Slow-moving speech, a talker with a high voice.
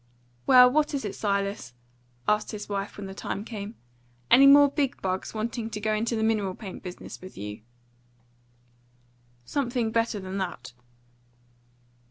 No: average, 150 wpm; high, 210 Hz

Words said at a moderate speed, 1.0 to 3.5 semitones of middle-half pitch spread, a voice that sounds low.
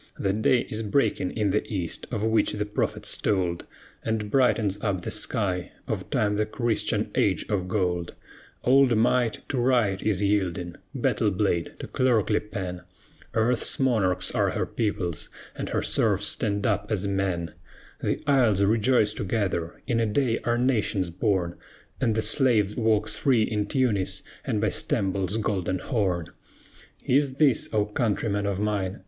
Yes: average, 155 wpm; average, 2.9 semitones; low, 105 Hz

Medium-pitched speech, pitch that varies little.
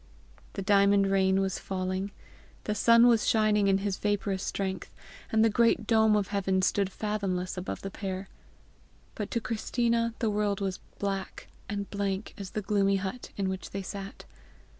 No: high, 200 Hz; narrow, 1.8 semitones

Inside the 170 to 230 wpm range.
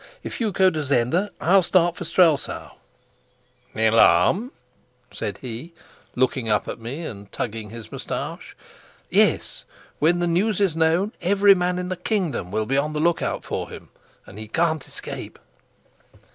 No: average, 160 wpm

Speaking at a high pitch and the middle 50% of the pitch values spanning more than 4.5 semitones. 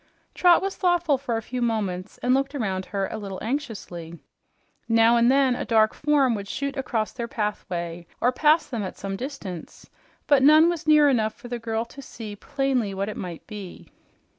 Yes: high, 235 Hz; wide, 5.4 semitones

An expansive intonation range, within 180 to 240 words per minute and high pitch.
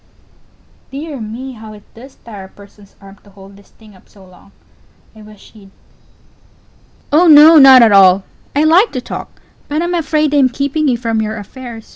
Yes: wide, 6.0 semitones; average, 190 wpm; high, 230 Hz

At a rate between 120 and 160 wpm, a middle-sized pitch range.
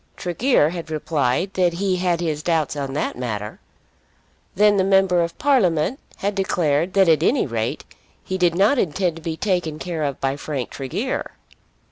No: average, 170 wpm; average, 4.2 semitones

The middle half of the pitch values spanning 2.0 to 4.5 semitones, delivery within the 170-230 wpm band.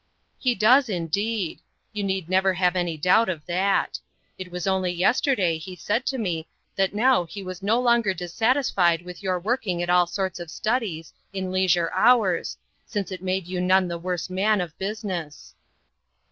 Yes: average, 3.1 semitones; average, 175 wpm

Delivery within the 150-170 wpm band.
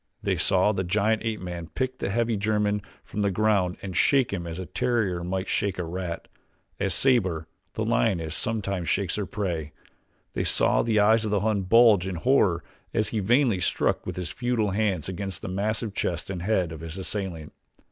No: average, 195 wpm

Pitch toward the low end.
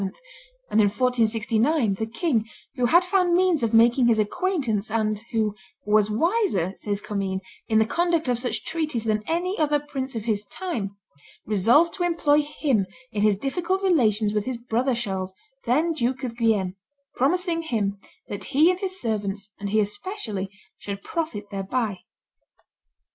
No: high, 235 Hz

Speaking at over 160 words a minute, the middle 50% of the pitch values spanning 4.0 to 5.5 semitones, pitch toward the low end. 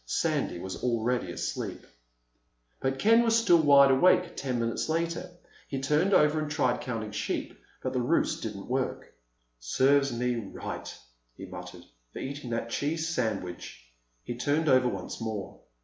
No: average, 150 wpm; average, 4.7 semitones; low, 130 Hz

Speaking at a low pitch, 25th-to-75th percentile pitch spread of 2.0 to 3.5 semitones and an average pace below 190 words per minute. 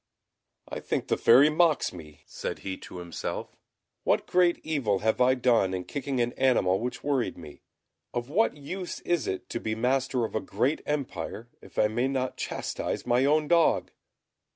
No: low, 125 Hz; average, 4.9 semitones; average, 175 wpm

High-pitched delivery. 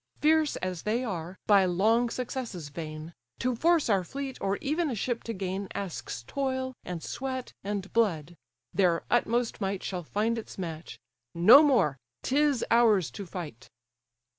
Yes: high, 205 Hz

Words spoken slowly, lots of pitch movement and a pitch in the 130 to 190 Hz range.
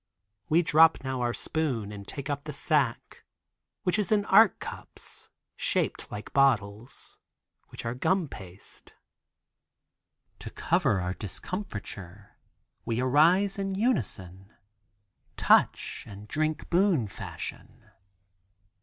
Yes: slow, 110 wpm; wide, 8.9 semitones; low, 135 Hz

